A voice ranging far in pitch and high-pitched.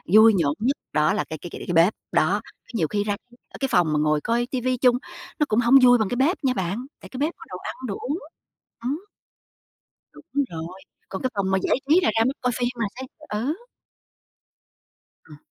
Yes: wide, 5.8 semitones; high, 230 Hz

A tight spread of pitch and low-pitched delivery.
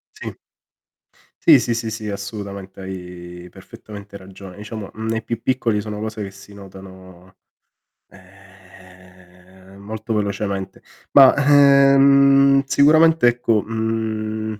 No: average, 3.1 semitones; low, 105 Hz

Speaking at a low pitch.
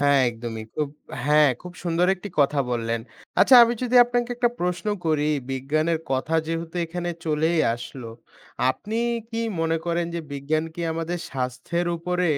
No: medium, 165 Hz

